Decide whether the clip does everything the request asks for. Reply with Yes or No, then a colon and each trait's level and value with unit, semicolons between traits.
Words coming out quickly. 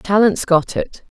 No: average, 150 wpm